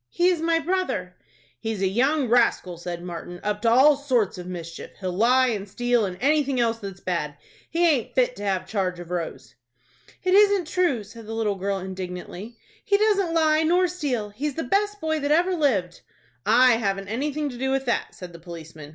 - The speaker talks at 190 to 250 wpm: Yes, average, 200 wpm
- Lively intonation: Yes, wide, 8.3 semitones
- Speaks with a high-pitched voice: Yes, high, 235 Hz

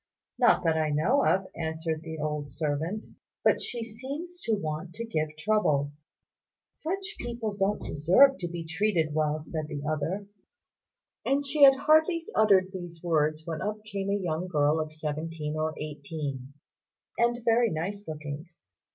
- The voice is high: No, medium, 165 Hz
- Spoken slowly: No, average, 155 wpm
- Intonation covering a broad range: Yes, wide, 5.9 semitones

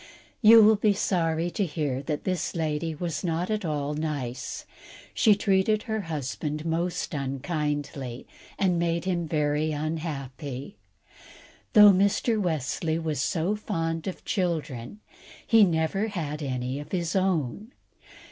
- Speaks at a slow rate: Yes, slow, 130 wpm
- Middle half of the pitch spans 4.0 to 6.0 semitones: Yes, average, 4.4 semitones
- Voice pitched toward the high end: No, medium, 165 Hz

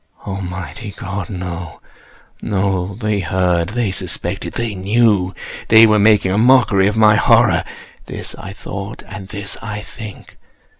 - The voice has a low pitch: Yes, low, 100 Hz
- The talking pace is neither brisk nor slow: No, slow, 110 wpm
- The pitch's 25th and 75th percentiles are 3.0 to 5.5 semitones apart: No, narrow, 2.5 semitones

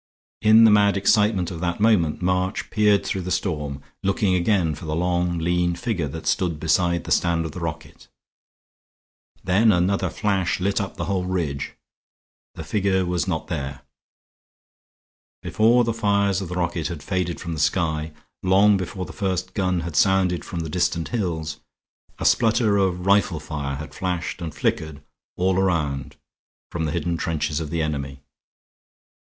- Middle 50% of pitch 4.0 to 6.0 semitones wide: No, average, 3.2 semitones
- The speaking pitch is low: Yes, very low, 90 Hz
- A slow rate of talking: No, average, 165 wpm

